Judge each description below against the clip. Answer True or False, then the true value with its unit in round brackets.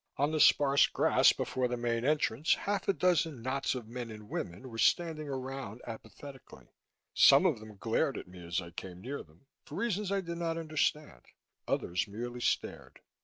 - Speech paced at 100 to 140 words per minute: False (180 wpm)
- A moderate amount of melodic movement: False (5.8 semitones)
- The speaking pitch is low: True (130 Hz)